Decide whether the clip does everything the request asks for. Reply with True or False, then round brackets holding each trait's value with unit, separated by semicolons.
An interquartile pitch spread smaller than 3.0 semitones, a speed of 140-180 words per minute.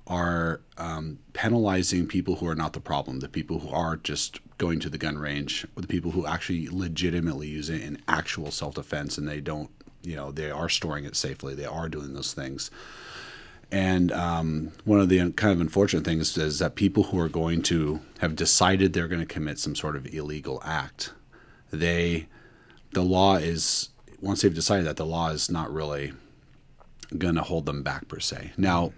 False (2.6 semitones; 195 wpm)